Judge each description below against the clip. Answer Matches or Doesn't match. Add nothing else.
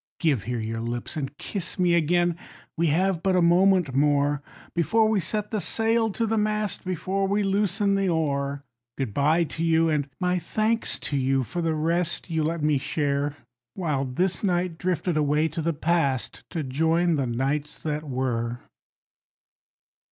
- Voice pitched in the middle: Matches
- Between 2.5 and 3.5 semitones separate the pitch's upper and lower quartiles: Doesn't match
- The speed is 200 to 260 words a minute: Doesn't match